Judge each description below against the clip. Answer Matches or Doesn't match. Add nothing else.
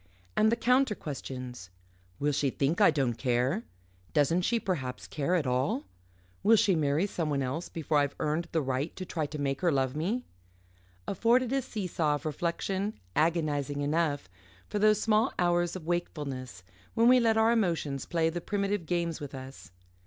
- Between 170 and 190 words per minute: Matches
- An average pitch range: Doesn't match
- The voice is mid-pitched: Matches